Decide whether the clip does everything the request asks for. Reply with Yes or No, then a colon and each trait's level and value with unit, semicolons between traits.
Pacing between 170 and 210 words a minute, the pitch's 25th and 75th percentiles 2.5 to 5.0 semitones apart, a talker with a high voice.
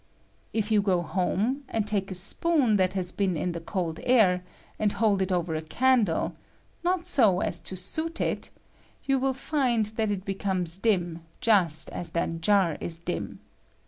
Yes: average, 190 wpm; average, 4.2 semitones; high, 195 Hz